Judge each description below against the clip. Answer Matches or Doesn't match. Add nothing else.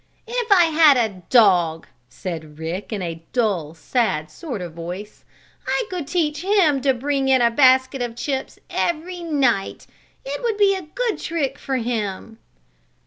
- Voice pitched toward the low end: Doesn't match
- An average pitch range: Doesn't match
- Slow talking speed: Doesn't match